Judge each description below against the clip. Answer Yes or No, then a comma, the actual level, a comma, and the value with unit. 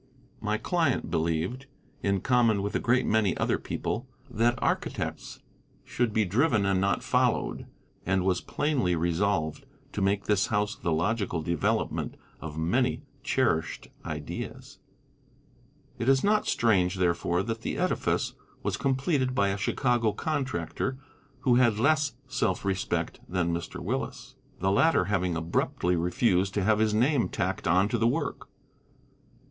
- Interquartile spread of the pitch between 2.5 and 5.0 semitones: No, wide, 5.5 semitones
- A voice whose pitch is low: Yes, low, 105 Hz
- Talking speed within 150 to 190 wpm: No, average, 140 wpm